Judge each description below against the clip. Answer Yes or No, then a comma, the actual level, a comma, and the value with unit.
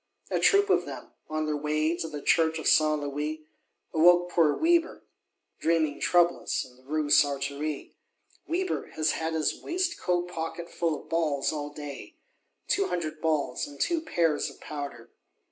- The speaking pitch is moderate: Yes, medium, 155 Hz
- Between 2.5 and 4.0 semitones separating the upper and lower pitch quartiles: Yes, average, 2.8 semitones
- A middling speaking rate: Yes, average, 160 wpm